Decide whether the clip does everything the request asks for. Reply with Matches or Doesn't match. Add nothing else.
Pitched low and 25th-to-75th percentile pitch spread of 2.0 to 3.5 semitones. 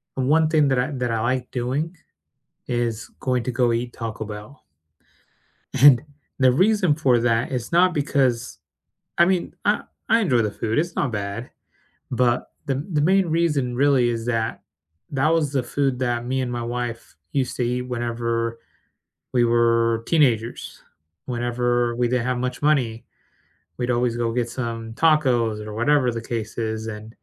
Matches